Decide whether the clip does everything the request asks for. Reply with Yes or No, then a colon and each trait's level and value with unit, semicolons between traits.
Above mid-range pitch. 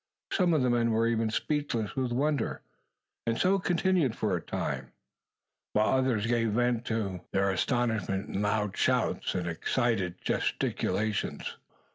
No: low, 115 Hz